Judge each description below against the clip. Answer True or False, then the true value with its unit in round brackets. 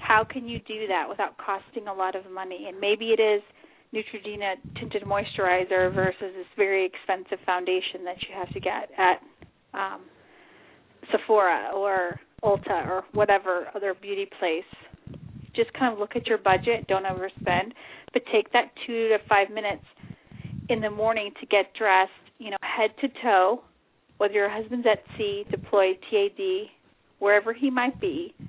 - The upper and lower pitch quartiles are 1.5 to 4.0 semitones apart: True (3.1 semitones)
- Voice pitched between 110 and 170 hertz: False (205 Hz)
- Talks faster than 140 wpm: True (165 wpm)